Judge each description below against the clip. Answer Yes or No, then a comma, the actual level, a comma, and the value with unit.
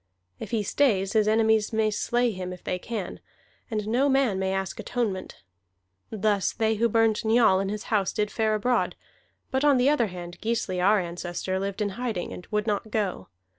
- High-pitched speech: Yes, high, 215 Hz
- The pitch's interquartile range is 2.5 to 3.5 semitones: Yes, average, 3.0 semitones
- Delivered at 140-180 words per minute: No, average, 190 wpm